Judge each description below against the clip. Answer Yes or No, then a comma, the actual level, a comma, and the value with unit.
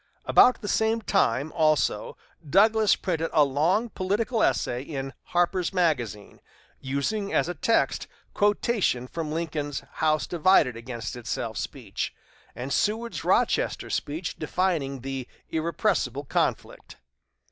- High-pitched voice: No, medium, 160 Hz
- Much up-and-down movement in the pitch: Yes, wide, 6.4 semitones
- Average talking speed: No, slow, 115 wpm